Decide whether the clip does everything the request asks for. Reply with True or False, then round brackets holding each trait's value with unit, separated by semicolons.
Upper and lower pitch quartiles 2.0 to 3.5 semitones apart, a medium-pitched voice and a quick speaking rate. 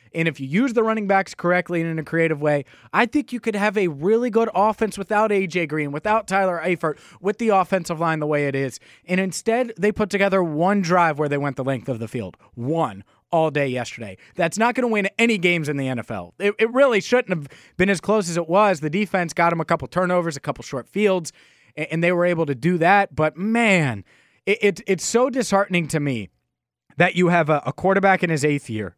False (5.1 semitones; 175 Hz; 235 wpm)